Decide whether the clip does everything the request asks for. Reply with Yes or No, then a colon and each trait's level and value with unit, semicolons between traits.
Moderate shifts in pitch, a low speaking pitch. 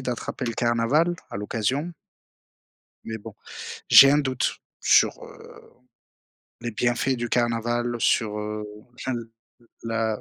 No: narrow, 2.3 semitones; low, 120 Hz